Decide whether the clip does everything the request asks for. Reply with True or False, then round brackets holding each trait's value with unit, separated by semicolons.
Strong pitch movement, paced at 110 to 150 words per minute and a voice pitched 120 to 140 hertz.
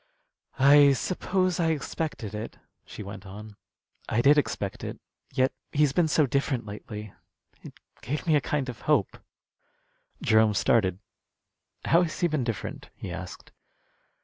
True (6.0 semitones; 145 wpm; 130 Hz)